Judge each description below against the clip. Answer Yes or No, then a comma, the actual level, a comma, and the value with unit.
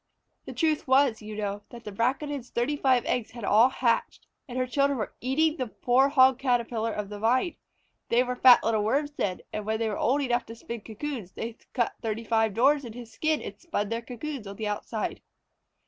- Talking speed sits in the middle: No, fast, 220 wpm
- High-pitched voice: Yes, high, 240 Hz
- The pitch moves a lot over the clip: No, average, 3.3 semitones